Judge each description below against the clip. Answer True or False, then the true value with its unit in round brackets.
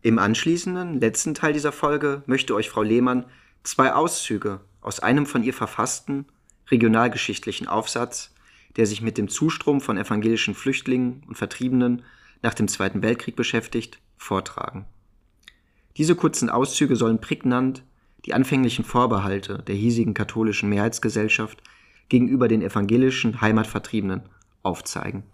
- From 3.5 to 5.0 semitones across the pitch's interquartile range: True (3.8 semitones)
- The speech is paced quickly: False (125 wpm)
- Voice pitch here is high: False (115 Hz)